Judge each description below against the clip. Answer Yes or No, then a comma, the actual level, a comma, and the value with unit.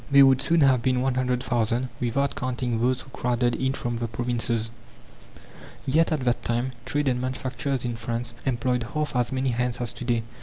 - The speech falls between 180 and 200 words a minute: Yes, average, 185 wpm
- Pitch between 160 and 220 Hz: No, low, 125 Hz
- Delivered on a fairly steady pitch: Yes, narrow, 1.6 semitones